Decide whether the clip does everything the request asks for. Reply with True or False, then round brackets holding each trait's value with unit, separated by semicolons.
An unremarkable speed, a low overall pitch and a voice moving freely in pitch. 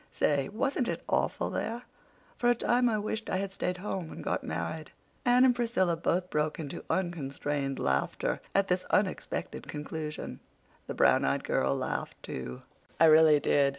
False (165 wpm; 175 Hz; 6.5 semitones)